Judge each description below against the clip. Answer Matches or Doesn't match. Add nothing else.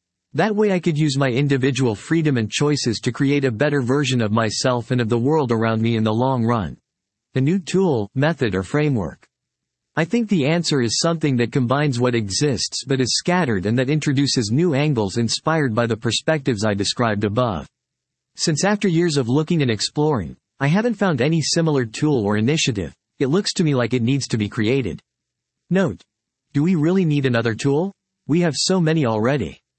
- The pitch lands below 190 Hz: Matches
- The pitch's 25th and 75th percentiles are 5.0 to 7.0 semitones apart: Matches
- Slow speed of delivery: Doesn't match